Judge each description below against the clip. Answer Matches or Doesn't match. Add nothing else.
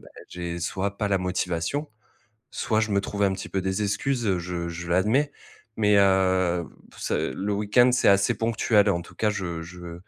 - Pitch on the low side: Matches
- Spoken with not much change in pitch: Doesn't match